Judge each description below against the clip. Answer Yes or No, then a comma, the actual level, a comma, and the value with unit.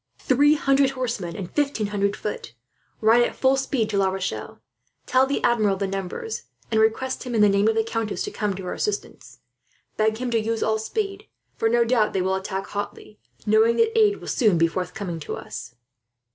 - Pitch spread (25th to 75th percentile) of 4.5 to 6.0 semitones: Yes, average, 4.8 semitones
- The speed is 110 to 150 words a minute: No, average, 200 wpm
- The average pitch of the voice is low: No, high, 220 Hz